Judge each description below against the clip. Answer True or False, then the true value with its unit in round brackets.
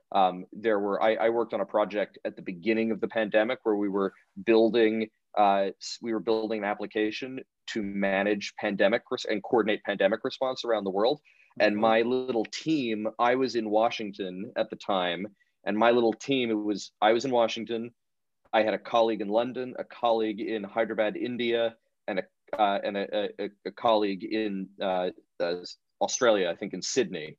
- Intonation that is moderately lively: False (2.0 semitones)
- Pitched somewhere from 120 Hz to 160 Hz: False (110 Hz)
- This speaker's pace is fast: False (185 wpm)